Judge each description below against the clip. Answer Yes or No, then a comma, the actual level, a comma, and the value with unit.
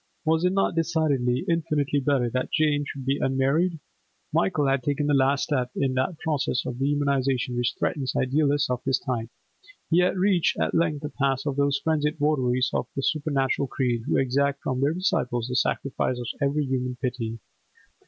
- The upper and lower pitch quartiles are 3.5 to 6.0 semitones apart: No, average, 2.7 semitones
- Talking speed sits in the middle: Yes, average, 180 wpm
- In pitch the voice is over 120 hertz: Yes, medium, 140 Hz